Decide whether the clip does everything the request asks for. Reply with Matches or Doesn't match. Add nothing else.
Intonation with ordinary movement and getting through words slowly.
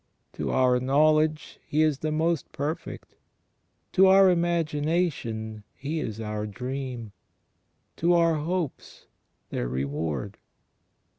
Doesn't match